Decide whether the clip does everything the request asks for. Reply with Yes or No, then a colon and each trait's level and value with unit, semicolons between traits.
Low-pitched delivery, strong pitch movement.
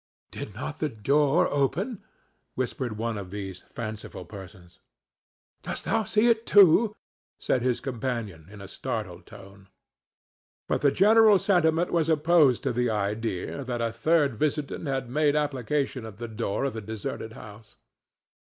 Yes: low, 130 Hz; wide, 6.2 semitones